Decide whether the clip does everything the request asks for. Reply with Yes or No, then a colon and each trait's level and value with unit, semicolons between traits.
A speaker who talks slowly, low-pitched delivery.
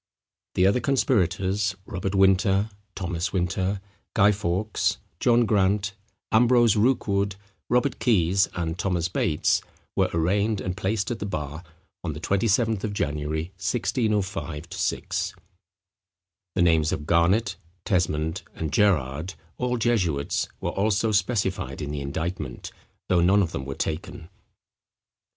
Yes: slow, 125 wpm; very low, 95 Hz